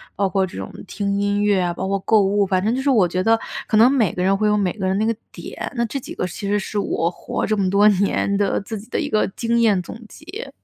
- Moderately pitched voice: No, high, 205 Hz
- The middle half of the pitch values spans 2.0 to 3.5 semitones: Yes, narrow, 2.6 semitones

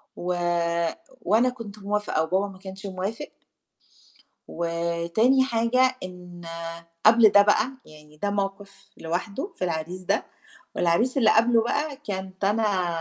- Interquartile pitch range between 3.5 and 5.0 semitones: Yes, average, 4.2 semitones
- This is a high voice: Yes, high, 200 Hz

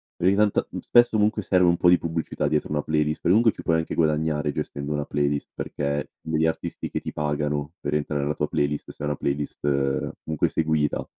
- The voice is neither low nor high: No, very low, 75 Hz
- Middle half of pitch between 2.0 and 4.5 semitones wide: Yes, narrow, 2.6 semitones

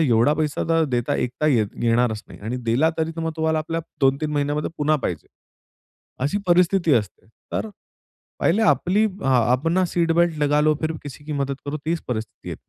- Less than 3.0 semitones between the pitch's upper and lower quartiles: No, average, 3.8 semitones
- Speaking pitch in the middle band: Yes, medium, 150 Hz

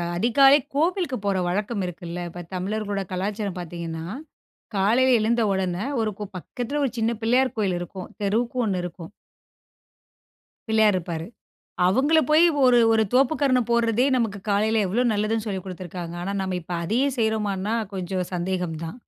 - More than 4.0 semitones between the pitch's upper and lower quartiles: Yes, average, 4.6 semitones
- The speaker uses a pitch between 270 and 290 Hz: No, high, 210 Hz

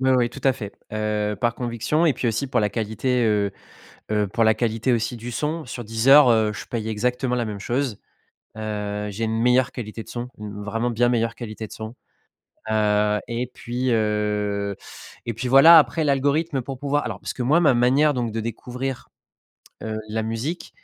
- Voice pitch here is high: No, low, 115 Hz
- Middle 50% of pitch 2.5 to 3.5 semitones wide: Yes, average, 3.0 semitones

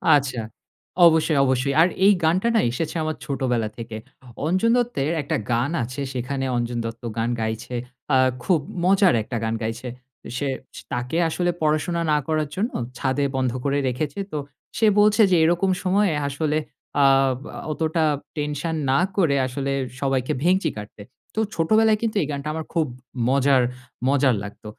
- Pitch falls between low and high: Yes, medium, 145 Hz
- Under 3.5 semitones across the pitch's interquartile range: No, average, 4.8 semitones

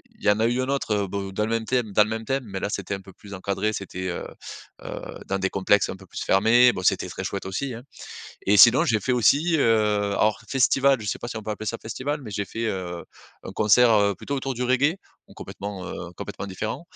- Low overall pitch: Yes, low, 110 Hz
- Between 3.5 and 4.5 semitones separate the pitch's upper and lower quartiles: Yes, average, 3.9 semitones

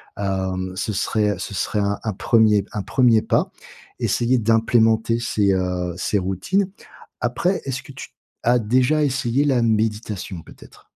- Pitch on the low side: Yes, low, 110 Hz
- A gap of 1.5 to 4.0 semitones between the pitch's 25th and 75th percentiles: Yes, average, 3.4 semitones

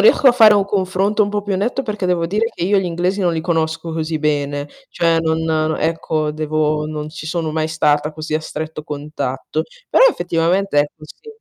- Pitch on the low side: No, medium, 160 Hz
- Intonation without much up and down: No, average, 3.8 semitones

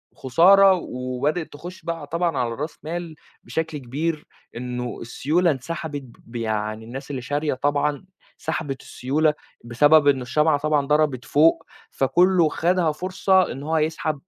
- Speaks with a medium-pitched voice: Yes, medium, 150 Hz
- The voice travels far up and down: No, average, 3.9 semitones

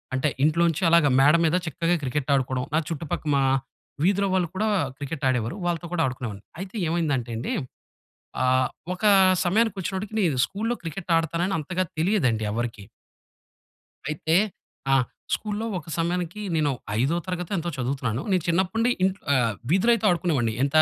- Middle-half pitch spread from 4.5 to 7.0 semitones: Yes, wide, 5.6 semitones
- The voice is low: No, medium, 165 Hz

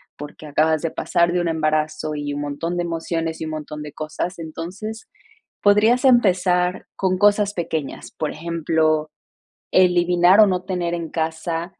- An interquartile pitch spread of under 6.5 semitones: Yes, average, 2.7 semitones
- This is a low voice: No, medium, 170 Hz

